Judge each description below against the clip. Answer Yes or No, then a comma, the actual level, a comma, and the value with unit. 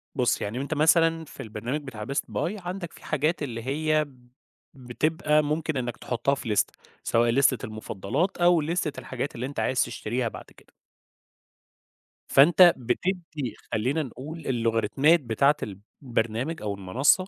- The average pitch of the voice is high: No, low, 135 Hz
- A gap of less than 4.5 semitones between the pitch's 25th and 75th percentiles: No, average, 4.9 semitones